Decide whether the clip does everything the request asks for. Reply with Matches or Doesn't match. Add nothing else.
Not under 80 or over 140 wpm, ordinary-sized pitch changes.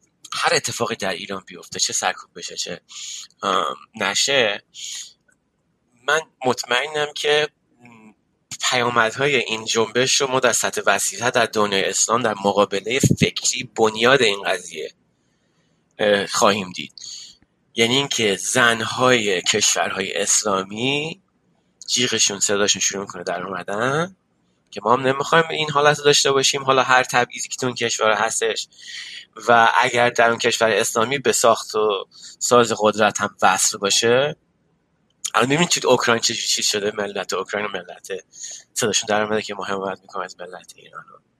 Matches